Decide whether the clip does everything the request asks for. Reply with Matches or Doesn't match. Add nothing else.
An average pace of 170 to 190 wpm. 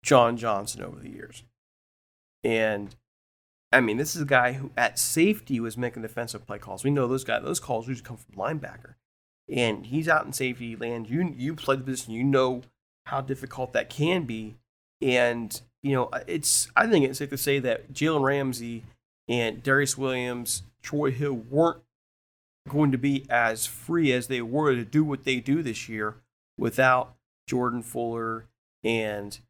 Matches